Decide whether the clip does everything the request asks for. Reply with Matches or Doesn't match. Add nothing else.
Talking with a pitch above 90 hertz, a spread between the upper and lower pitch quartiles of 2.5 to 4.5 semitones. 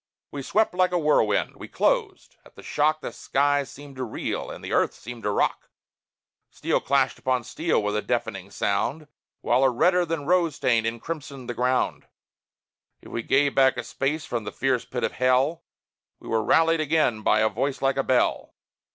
Matches